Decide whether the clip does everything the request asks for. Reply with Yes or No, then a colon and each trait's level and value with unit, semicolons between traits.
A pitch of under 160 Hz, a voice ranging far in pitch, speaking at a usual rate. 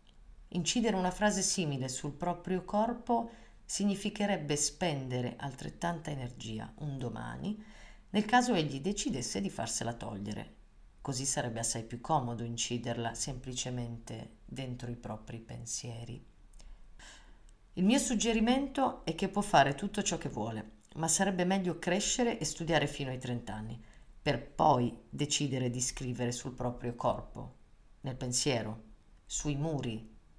Yes: low, 135 Hz; wide, 7.5 semitones; average, 125 wpm